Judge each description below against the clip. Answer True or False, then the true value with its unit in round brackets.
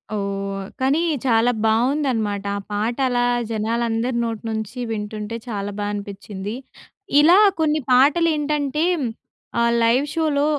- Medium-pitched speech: False (230 Hz)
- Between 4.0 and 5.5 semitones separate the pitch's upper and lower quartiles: True (4.9 semitones)